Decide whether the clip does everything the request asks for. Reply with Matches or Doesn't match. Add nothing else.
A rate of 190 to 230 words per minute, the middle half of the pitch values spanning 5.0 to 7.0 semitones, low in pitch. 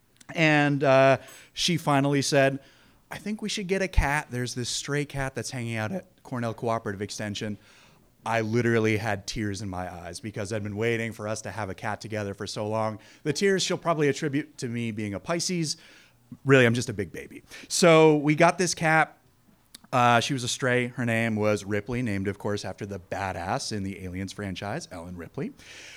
Matches